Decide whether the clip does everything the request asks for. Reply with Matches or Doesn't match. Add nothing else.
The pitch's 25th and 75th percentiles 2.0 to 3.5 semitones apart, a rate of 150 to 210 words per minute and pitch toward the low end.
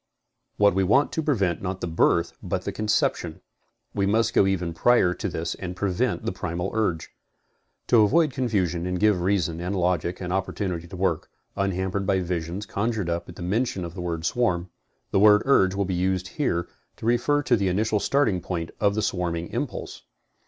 Matches